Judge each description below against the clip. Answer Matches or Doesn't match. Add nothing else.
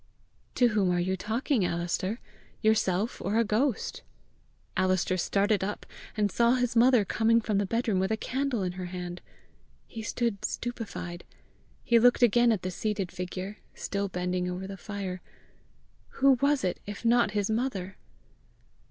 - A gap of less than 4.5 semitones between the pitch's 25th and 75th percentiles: Matches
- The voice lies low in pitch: Doesn't match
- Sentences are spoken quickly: Doesn't match